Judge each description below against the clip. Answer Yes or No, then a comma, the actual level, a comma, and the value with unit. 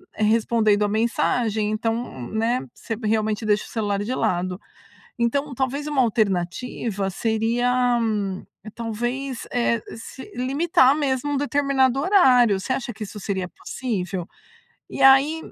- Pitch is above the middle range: Yes, high, 230 Hz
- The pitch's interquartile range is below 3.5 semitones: No, average, 3.8 semitones